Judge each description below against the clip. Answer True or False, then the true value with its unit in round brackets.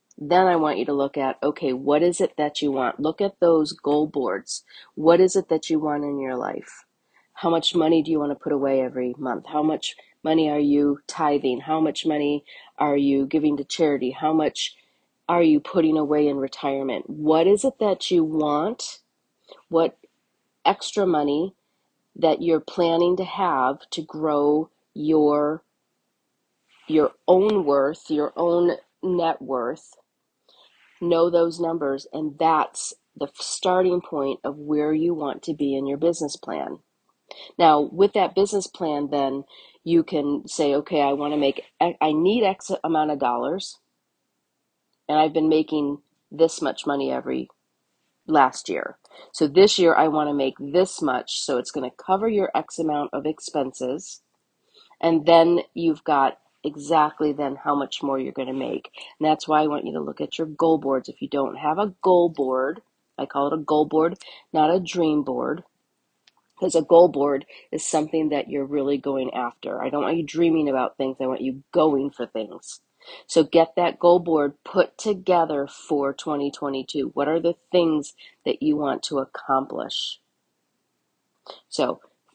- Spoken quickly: False (175 wpm)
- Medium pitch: True (150 Hz)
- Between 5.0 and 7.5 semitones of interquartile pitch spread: False (2.9 semitones)